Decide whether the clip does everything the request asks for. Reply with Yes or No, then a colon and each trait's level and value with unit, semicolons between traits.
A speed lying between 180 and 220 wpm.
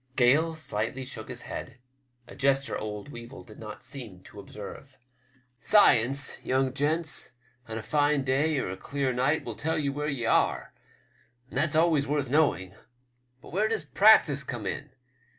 No: average, 165 wpm